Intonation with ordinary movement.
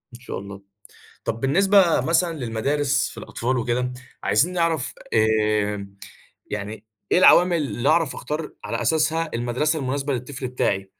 No: wide, 5.8 semitones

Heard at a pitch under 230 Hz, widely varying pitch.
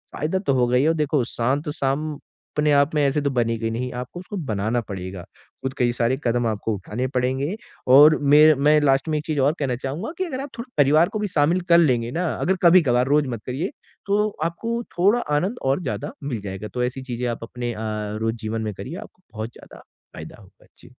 No: medium, 140 Hz; average, 4.8 semitones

